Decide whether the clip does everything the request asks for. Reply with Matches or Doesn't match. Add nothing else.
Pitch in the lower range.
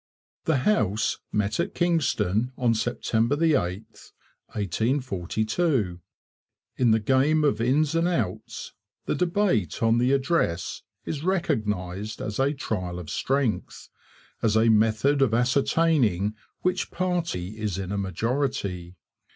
Matches